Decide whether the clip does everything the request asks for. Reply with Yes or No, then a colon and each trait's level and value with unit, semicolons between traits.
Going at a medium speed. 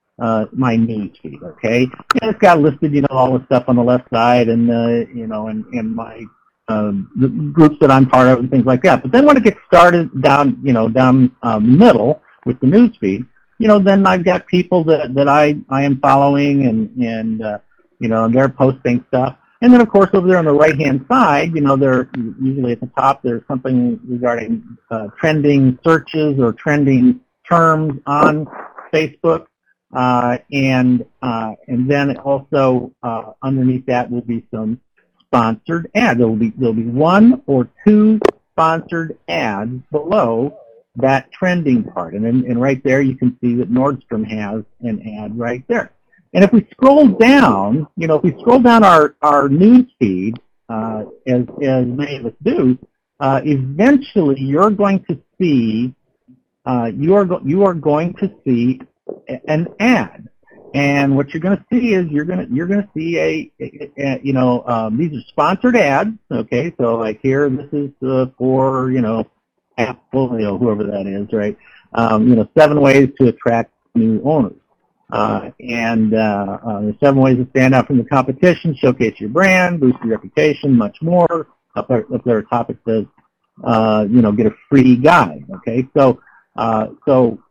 Yes: average, 180 wpm